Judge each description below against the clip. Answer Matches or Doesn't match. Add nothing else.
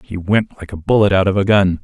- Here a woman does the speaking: Doesn't match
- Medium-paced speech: Doesn't match